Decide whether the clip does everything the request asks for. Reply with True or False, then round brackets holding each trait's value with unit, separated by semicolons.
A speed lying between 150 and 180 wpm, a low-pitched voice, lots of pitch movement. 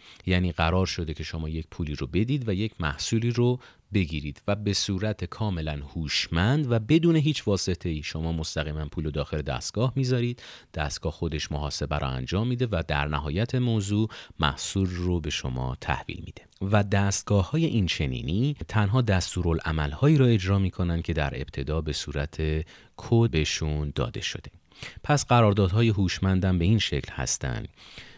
True (155 wpm; 90 Hz; 5.8 semitones)